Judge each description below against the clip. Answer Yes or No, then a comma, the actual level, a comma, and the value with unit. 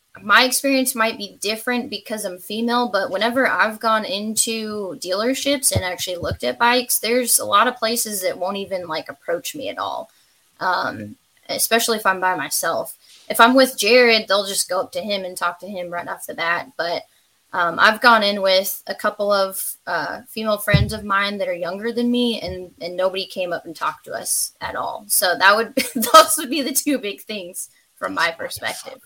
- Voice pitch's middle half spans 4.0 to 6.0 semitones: Yes, average, 4.3 semitones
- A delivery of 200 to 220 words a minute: Yes, fast, 205 wpm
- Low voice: No, high, 210 Hz